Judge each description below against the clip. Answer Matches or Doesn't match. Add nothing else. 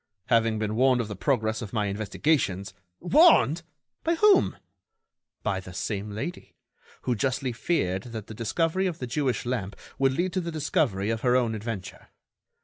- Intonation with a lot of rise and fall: Matches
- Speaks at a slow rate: Doesn't match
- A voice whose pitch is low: Matches